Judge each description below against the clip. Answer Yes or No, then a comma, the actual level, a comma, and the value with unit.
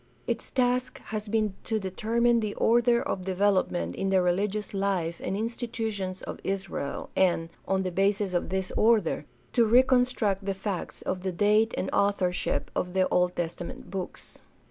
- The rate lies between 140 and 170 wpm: Yes, average, 155 wpm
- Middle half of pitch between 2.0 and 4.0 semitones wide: Yes, average, 3.2 semitones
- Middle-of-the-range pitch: No, high, 195 Hz